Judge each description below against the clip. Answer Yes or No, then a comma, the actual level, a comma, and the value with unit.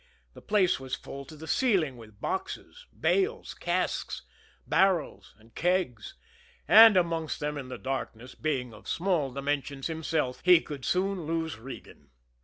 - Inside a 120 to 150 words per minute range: Yes, average, 145 wpm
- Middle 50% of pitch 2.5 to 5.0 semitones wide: No, wide, 5.6 semitones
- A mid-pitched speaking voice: Yes, medium, 155 Hz